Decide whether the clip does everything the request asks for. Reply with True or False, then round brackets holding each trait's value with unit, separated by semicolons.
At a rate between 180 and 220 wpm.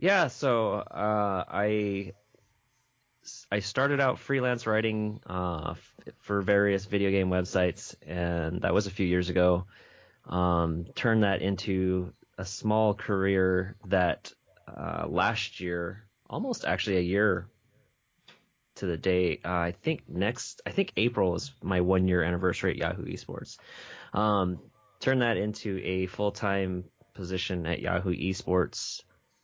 False (135 wpm)